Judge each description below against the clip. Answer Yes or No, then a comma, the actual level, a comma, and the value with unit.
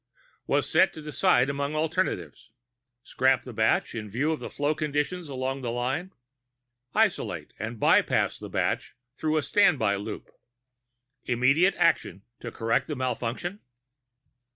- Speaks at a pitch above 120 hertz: Yes, low, 135 Hz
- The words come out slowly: Yes, slow, 130 wpm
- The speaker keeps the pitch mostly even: No, average, 4.3 semitones